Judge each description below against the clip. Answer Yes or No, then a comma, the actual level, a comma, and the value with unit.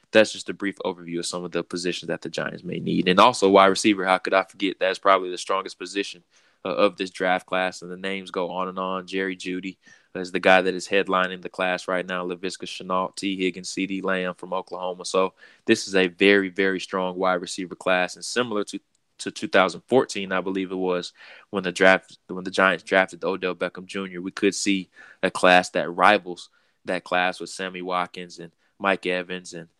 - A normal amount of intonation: No, narrow, 1.1 semitones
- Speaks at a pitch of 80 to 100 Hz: Yes, very low, 95 Hz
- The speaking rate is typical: No, fast, 215 wpm